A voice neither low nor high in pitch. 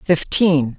Yes: medium, 155 Hz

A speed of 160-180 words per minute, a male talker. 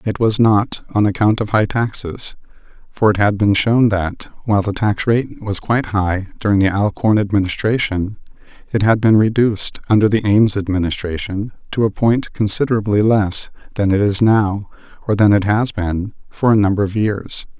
Yes: average, 175 wpm; male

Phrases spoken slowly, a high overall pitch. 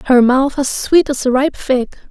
No: fast, 230 wpm; very high, 265 Hz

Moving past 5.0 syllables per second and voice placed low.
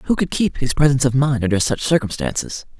Yes: 6.0 syllables/s; low, 130 Hz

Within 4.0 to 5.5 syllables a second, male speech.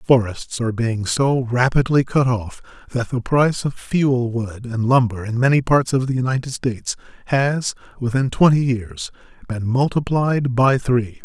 Yes: 4.5 syllables/s; male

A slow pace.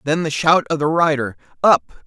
No: fast, 205 wpm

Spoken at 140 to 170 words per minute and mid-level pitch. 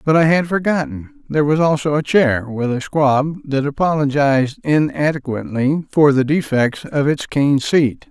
Yes: average, 155 wpm; medium, 145 Hz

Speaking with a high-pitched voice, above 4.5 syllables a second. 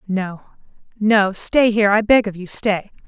No: high, 205 Hz; 4.4 syllables/s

